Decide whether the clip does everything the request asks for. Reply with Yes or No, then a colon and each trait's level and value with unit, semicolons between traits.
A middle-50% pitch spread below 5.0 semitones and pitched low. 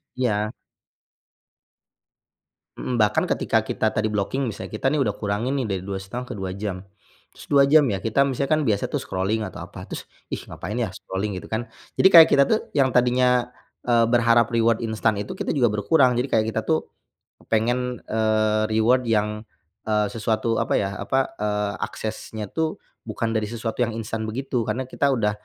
Yes: average, 2.8 semitones; low, 110 Hz